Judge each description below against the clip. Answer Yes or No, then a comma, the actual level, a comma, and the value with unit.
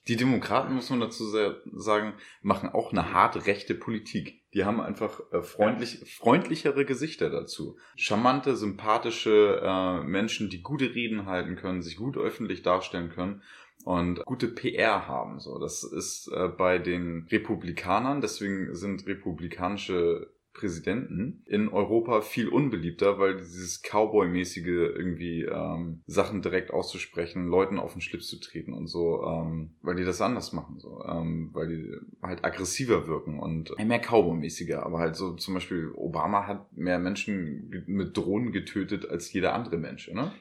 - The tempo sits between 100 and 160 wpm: Yes, average, 150 wpm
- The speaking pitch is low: Yes, very low, 90 Hz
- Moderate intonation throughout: Yes, average, 3.3 semitones